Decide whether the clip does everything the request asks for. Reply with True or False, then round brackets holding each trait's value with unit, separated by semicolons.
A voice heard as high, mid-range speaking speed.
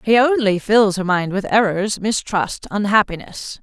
True (205 Hz; 150 wpm)